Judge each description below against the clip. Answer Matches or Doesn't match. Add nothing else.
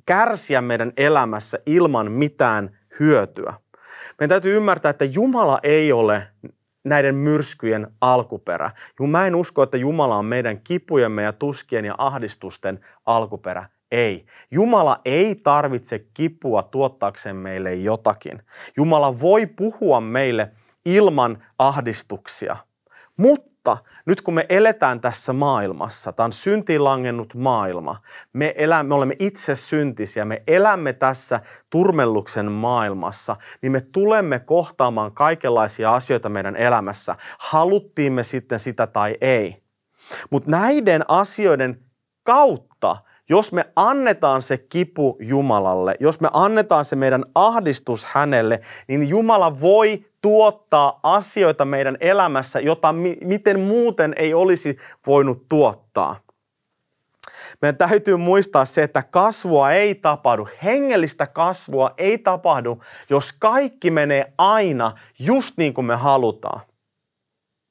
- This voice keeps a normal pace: Matches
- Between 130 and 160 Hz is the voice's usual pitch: Matches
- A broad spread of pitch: Matches